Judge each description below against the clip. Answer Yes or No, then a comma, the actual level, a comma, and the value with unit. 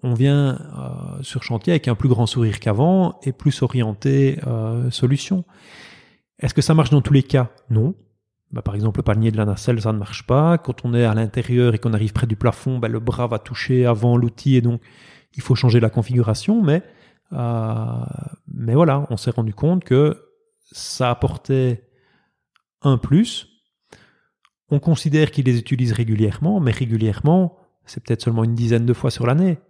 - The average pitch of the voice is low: Yes, low, 125 Hz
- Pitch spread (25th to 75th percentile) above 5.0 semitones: No, average, 3.7 semitones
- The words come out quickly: No, average, 185 wpm